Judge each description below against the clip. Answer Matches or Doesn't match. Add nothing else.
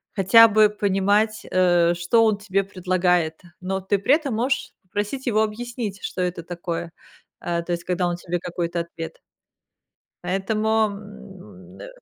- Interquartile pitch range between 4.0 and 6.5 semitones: Doesn't match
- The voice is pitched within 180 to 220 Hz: Matches